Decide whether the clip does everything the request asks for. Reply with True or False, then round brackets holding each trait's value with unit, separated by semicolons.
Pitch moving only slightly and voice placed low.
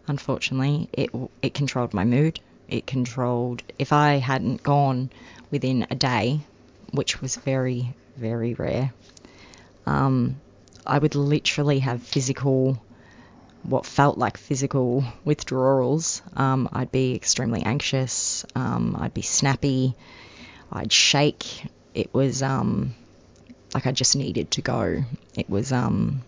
True (2.1 semitones; 130 Hz)